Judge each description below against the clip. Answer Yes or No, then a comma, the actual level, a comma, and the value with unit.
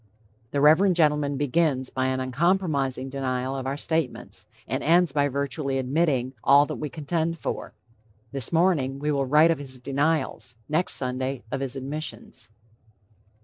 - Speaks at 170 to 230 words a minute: No, average, 150 wpm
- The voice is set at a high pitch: No, medium, 140 Hz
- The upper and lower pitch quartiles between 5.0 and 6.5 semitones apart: No, average, 3.1 semitones